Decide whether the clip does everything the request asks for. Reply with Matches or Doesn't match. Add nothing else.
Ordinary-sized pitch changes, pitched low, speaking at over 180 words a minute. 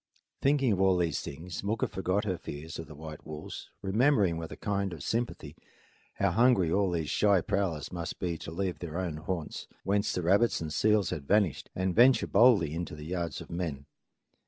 Matches